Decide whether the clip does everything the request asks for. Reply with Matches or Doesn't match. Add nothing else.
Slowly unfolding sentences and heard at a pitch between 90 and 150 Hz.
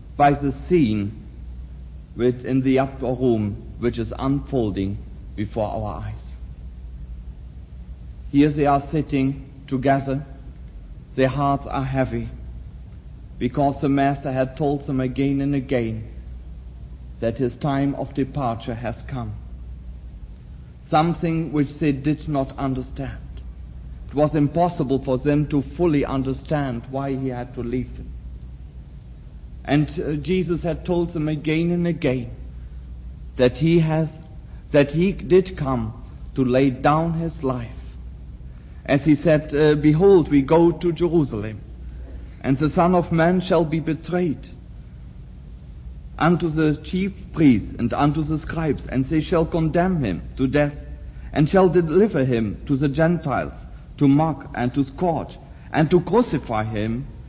Matches